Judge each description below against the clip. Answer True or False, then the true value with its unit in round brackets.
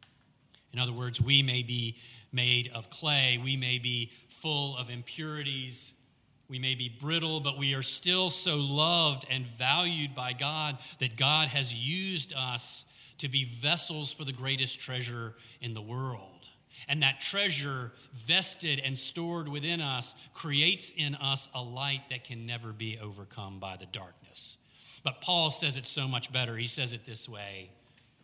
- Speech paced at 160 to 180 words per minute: True (165 wpm)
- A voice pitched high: False (130 Hz)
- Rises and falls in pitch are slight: False (3.2 semitones)